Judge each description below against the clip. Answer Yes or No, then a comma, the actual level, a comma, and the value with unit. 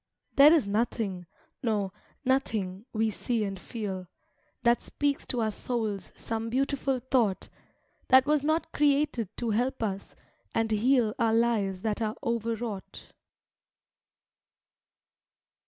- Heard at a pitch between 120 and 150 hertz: No, high, 230 Hz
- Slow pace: Yes, slow, 120 wpm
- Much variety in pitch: No, average, 3.7 semitones